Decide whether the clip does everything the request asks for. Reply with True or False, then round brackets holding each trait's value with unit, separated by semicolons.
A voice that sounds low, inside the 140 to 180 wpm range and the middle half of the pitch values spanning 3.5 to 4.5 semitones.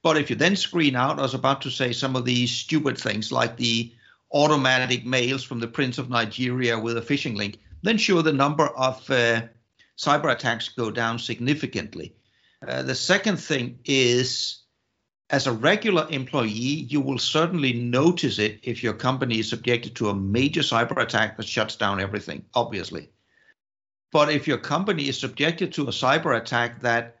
True (125 Hz; 175 wpm; 3.8 semitones)